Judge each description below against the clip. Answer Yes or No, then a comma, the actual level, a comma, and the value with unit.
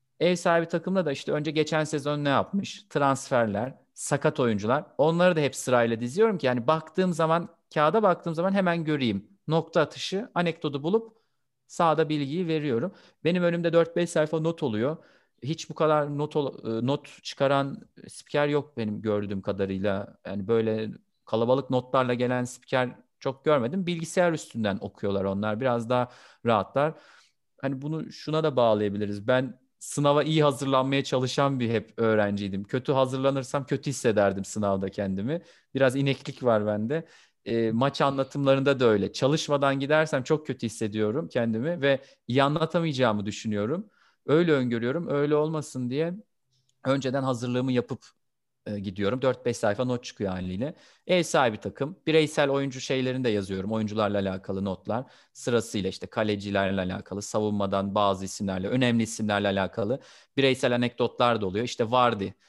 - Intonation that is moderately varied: No, wide, 5.8 semitones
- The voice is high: No, low, 130 Hz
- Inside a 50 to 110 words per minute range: No, fast, 140 wpm